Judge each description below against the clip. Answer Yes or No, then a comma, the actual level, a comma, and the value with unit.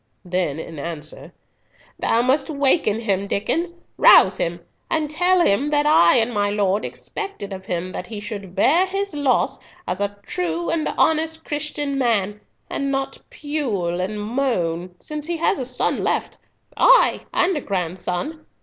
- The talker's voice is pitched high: Yes, high, 225 Hz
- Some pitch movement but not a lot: No, wide, 8.3 semitones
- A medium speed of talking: Yes, average, 155 wpm